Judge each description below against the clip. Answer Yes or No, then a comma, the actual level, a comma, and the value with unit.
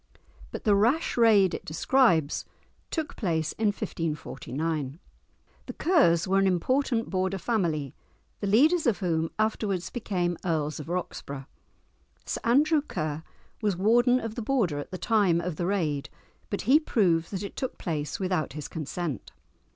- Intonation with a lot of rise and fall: Yes, wide, 5.8 semitones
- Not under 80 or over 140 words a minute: No, average, 150 wpm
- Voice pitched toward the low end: No, high, 190 Hz